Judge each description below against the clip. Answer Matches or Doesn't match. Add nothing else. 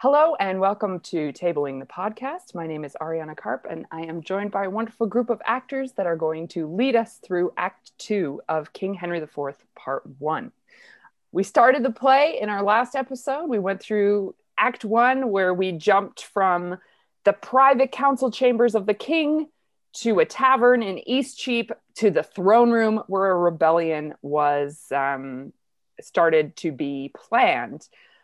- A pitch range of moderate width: Doesn't match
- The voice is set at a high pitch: Matches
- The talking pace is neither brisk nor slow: Matches